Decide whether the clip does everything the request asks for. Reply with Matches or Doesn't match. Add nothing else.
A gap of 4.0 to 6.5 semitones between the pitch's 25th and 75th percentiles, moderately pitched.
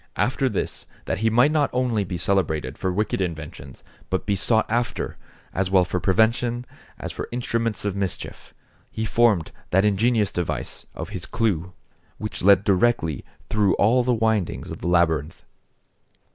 Doesn't match